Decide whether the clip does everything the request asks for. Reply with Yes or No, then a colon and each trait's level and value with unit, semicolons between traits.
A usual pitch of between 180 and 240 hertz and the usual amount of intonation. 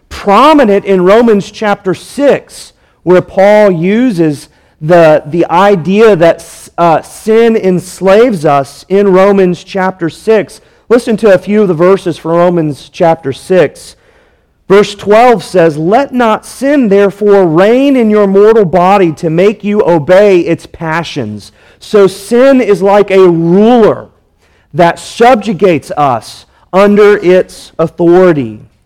Yes: high, 190 Hz; average, 3.9 semitones